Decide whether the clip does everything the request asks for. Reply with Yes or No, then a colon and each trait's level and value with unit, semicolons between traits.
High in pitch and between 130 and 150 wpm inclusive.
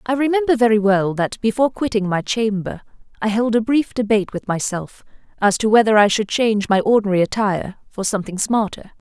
No: high, 215 Hz; average, 185 wpm